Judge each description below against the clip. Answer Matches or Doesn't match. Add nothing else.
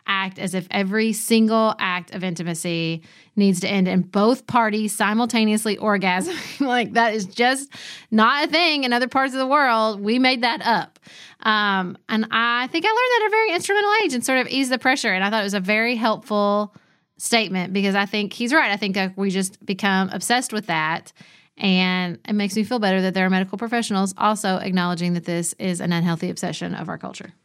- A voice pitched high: Matches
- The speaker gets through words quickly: Matches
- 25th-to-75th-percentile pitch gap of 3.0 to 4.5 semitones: Matches